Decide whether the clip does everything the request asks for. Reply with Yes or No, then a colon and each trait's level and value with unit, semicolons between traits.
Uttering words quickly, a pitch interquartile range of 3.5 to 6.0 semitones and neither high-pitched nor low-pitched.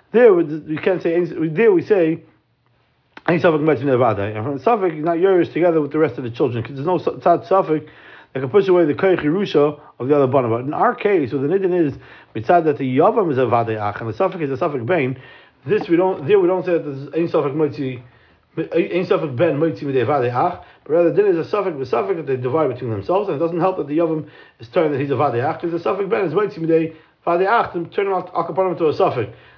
Yes: fast, 245 wpm; average, 4.8 semitones; medium, 160 Hz